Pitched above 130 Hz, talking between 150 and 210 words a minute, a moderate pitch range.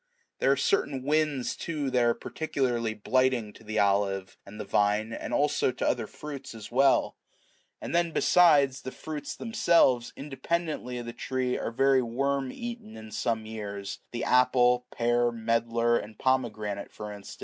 No: low, 125 Hz; average, 165 wpm; average, 3.8 semitones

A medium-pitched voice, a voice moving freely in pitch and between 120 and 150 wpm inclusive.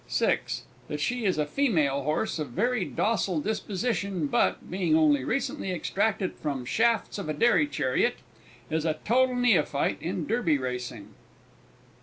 Yes: medium, 180 Hz; wide, 7.5 semitones; average, 140 wpm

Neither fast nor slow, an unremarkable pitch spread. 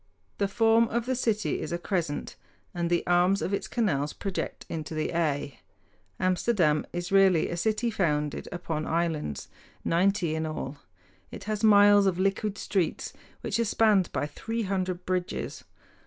Yes: average, 155 wpm; average, 3.9 semitones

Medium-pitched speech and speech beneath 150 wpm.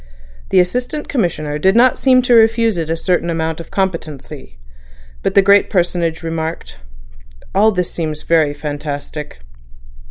Yes: medium, 170 Hz; average, 140 wpm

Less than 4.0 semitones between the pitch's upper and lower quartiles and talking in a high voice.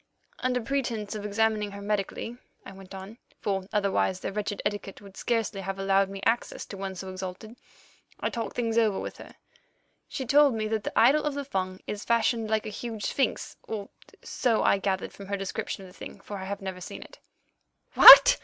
Yes: average, 2.8 semitones; high, 205 Hz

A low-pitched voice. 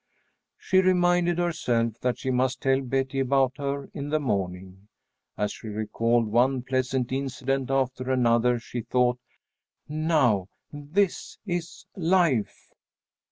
Yes: low, 130 Hz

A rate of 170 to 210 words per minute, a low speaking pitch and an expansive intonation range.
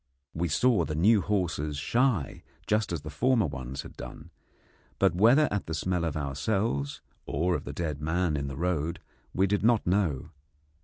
Yes: average, 175 wpm; very low, 85 Hz; wide, 5.8 semitones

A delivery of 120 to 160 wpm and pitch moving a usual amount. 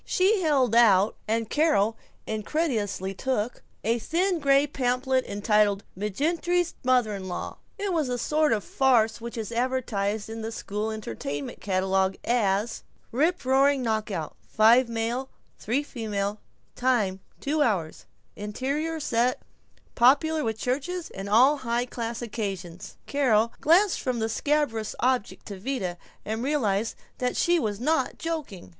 Yes: slow, 135 wpm; average, 5.0 semitones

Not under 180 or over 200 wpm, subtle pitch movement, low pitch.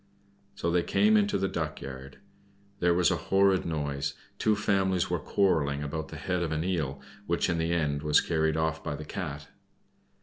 No: average, 190 wpm; average, 3.8 semitones; very low, 80 Hz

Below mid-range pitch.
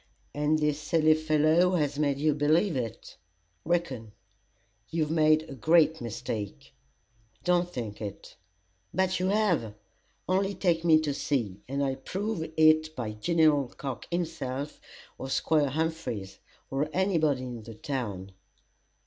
No: medium, 155 Hz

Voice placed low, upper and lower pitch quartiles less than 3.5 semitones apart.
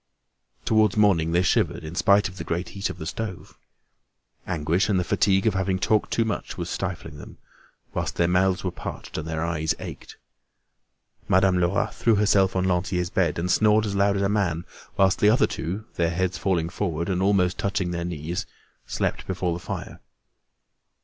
Yes: very low, 95 Hz; narrow, 2.6 semitones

